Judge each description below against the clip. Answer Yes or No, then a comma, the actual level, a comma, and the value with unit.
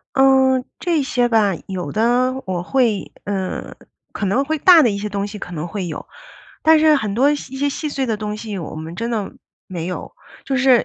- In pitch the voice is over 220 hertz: Yes, high, 230 Hz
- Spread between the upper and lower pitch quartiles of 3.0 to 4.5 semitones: No, average, 5.3 semitones